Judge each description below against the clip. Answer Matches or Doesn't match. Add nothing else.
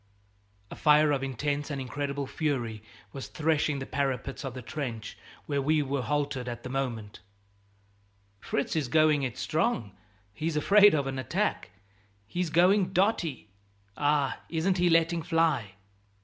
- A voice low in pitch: Doesn't match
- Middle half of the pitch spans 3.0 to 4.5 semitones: Matches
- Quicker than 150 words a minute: Doesn't match